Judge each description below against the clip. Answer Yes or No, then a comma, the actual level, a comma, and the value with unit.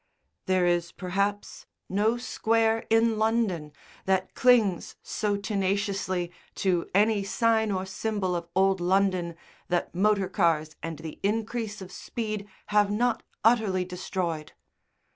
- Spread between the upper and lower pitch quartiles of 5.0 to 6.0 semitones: No, average, 3.2 semitones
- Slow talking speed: Yes, slow, 125 wpm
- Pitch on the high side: Yes, high, 195 Hz